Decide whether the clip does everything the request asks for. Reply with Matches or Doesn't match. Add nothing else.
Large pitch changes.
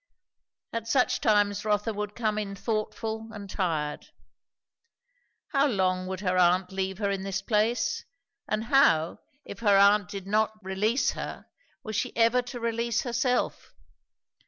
Doesn't match